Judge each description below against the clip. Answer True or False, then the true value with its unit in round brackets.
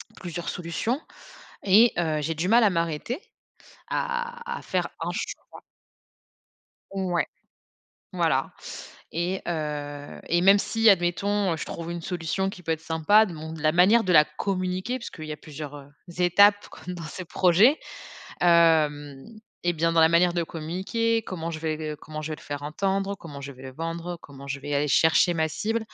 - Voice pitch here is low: False (170 Hz)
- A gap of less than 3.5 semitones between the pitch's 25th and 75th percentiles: False (3.8 semitones)